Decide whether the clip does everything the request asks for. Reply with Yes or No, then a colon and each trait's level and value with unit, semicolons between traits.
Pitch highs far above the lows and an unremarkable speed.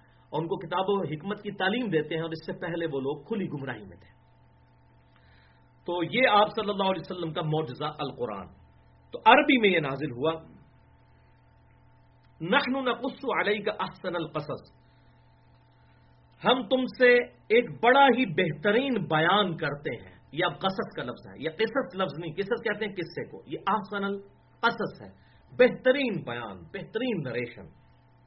Yes: wide, 6.8 semitones; average, 155 wpm